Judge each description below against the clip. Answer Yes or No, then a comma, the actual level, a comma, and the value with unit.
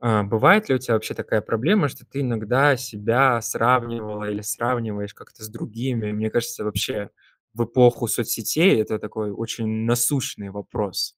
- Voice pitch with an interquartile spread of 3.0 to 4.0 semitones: No, narrow, 2.6 semitones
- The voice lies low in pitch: Yes, low, 115 Hz